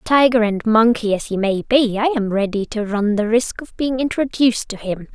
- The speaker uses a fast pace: Yes, fast, 220 wpm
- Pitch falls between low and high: No, high, 225 Hz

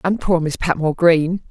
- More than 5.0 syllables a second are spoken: Yes, 5.2 syllables/s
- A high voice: No, medium, 170 Hz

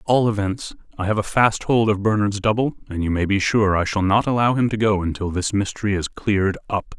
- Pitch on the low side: Yes, low, 105 Hz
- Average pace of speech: No, fast, 250 wpm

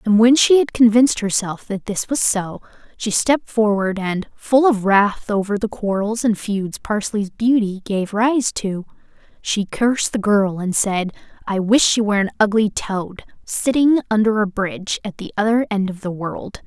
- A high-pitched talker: Yes, high, 210 Hz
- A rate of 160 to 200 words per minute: Yes, average, 185 wpm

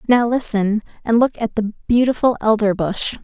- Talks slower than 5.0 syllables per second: Yes, 4.6 syllables/s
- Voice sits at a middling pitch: No, high, 220 Hz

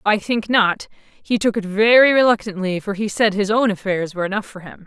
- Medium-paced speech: No, fast, 220 wpm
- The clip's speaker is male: No, female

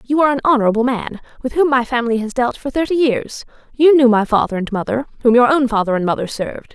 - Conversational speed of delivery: No, fast, 240 wpm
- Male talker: No, female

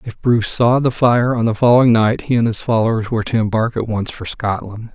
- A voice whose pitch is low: Yes, low, 115 Hz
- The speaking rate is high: Yes, fast, 245 wpm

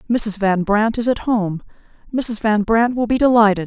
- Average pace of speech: Yes, average, 195 wpm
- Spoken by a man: No, female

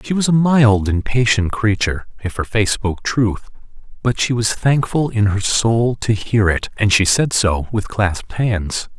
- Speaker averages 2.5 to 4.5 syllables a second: Yes, 4.4 syllables/s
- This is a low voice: Yes, low, 110 Hz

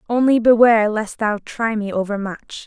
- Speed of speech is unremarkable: Yes, average, 160 wpm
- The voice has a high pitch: Yes, high, 220 Hz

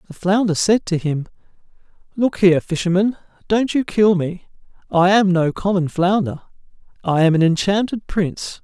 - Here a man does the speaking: Yes, male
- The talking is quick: No, average, 155 wpm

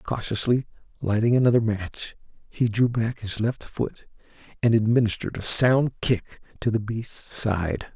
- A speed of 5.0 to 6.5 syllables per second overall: No, 4.4 syllables/s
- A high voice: No, low, 110 Hz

